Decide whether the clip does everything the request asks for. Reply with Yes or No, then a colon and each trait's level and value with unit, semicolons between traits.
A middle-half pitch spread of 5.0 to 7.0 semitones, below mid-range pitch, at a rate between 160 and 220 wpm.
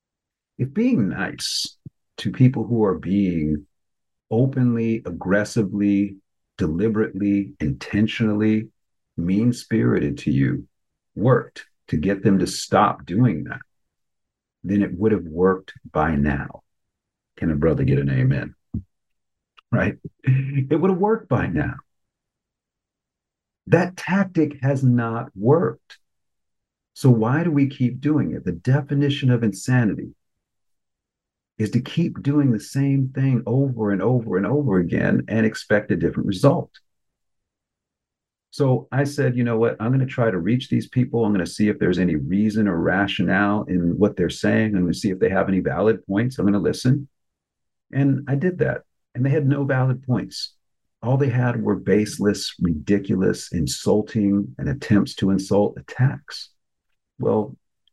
No: average, 5.3 semitones; low, 110 Hz; average, 150 wpm